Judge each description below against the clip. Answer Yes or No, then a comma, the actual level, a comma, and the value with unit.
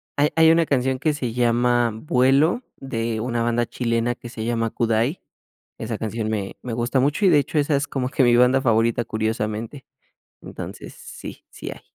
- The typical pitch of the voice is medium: No, low, 120 Hz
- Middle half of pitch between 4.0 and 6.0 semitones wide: No, average, 3.5 semitones